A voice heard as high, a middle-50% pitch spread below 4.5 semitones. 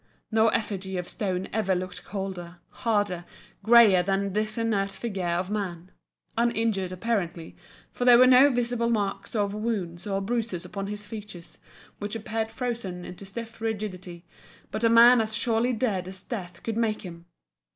Yes: high, 205 Hz; average, 3.6 semitones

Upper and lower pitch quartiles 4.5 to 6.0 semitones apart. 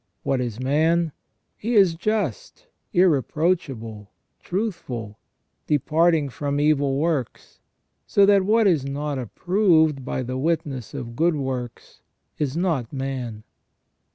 Yes: average, 5.0 semitones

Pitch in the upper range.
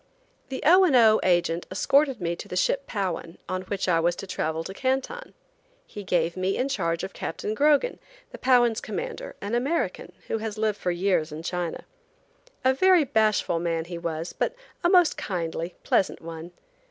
Yes: high, 195 Hz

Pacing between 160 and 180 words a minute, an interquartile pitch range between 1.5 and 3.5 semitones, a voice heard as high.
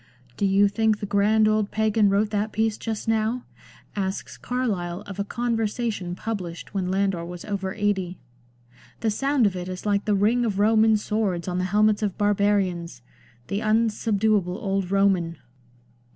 Yes: average, 165 wpm; narrow, 2.4 semitones; high, 205 Hz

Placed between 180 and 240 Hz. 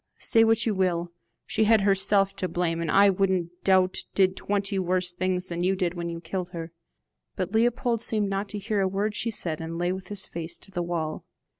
Yes: high, 190 Hz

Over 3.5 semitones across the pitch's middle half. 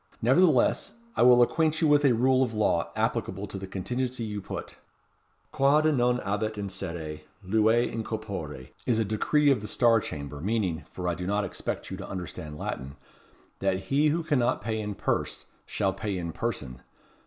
Yes: average, 4.9 semitones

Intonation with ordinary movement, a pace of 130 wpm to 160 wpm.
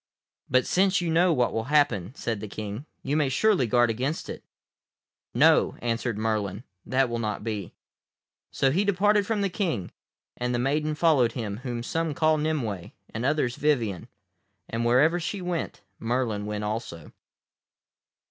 No: wide, 5.9 semitones; average, 155 wpm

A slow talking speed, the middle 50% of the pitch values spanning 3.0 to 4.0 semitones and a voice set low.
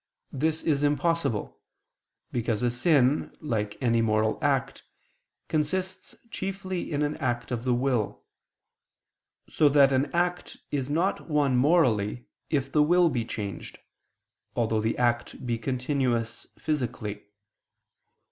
No: slow, 120 wpm; average, 4.6 semitones; low, 130 Hz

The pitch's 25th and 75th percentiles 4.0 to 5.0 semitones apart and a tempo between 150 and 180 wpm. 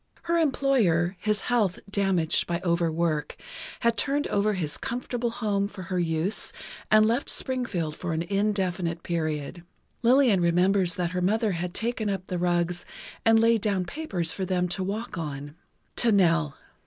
Yes: average, 4.4 semitones; average, 160 wpm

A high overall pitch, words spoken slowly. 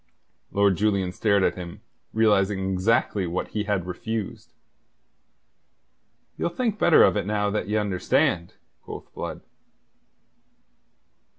No: low, 100 Hz; slow, 115 wpm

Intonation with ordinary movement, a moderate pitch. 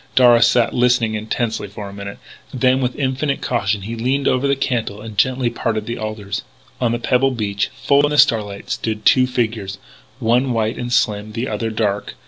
No: average, 3.1 semitones; low, 115 Hz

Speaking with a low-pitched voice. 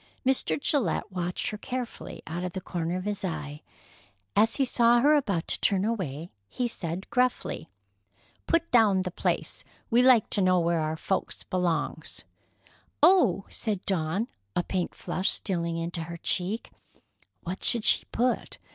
No: medium, 185 Hz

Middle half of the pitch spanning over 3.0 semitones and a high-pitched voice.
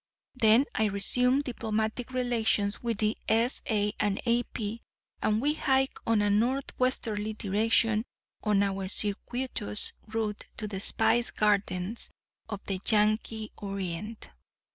No: narrow, 2.4 semitones; high, 220 Hz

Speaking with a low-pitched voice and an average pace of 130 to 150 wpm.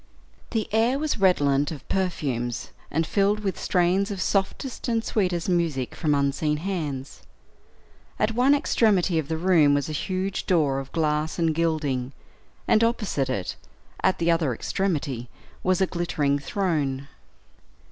No: medium, 165 Hz; average, 145 wpm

